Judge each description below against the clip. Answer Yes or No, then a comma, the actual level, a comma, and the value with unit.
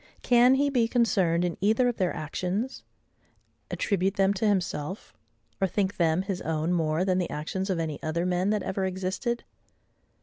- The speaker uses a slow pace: No, average, 170 wpm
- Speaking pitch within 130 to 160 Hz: No, high, 190 Hz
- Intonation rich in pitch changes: No, average, 3.7 semitones